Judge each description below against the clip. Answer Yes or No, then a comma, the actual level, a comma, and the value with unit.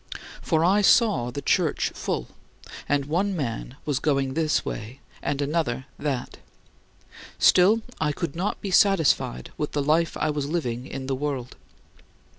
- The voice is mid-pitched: Yes, medium, 150 Hz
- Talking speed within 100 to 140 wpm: No, average, 155 wpm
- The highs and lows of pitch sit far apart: No, average, 4.0 semitones